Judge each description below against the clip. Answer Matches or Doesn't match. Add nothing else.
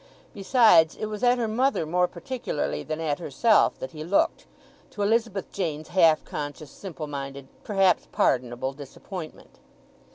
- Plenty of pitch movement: Matches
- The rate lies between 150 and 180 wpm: Doesn't match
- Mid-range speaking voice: Matches